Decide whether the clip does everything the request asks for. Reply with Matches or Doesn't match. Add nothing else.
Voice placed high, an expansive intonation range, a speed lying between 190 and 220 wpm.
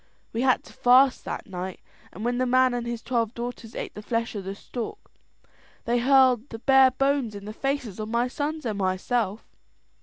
Doesn't match